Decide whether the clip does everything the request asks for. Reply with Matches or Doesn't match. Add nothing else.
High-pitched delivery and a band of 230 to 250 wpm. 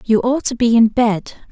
Matches